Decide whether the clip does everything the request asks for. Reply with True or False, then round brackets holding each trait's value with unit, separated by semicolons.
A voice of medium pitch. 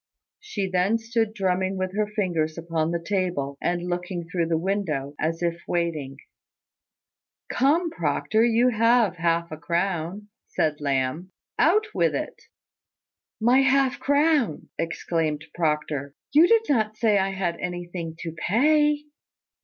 True (180 Hz)